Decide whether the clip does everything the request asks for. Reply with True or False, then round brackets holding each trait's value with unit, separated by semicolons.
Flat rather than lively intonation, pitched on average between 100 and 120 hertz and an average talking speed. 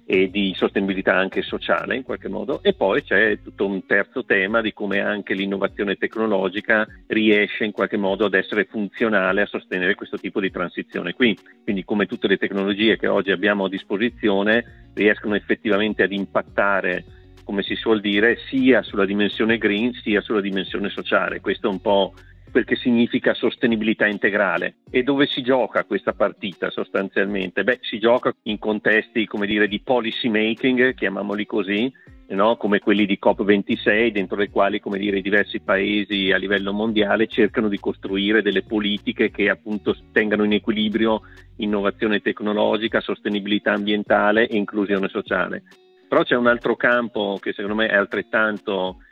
True (2.0 semitones; 105 Hz; 160 wpm)